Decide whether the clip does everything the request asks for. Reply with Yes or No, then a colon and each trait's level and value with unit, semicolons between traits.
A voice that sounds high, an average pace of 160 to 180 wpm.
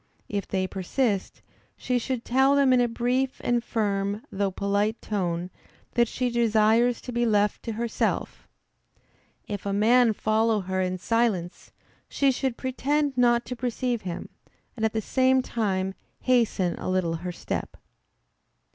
No: high, 225 Hz; average, 150 wpm